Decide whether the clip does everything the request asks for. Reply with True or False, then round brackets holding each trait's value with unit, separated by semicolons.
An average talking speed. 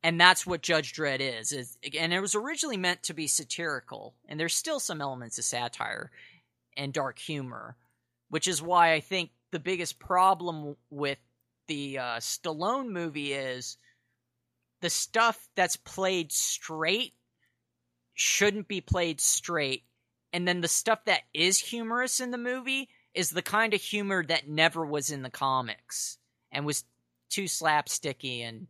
True (155 wpm)